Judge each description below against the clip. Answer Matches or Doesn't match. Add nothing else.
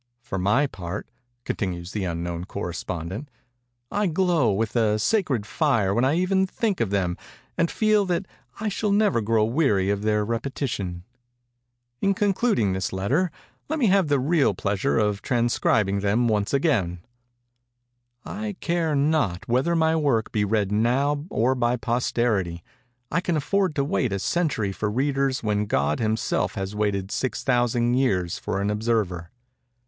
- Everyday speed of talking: Matches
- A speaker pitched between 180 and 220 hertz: Doesn't match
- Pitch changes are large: Matches